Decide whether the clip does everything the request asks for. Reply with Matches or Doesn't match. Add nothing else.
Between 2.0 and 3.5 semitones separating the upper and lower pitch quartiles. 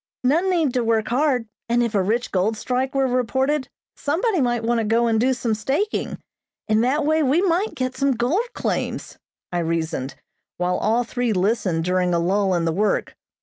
Doesn't match